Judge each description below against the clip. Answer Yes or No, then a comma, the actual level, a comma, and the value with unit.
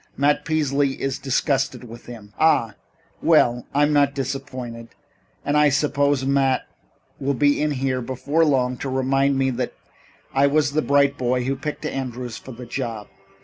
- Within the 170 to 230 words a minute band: No, average, 160 wpm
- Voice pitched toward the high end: No, low, 135 Hz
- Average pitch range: No, narrow, 2.1 semitones